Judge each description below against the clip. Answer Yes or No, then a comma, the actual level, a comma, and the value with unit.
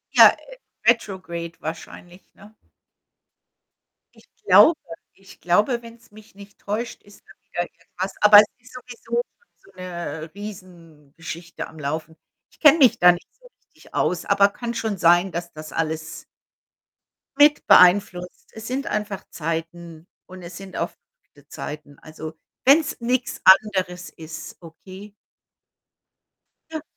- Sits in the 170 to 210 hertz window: Yes, medium, 185 Hz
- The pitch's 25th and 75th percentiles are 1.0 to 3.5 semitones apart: No, average, 4.4 semitones